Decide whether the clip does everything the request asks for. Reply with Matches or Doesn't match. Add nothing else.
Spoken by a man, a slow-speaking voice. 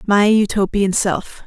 Doesn't match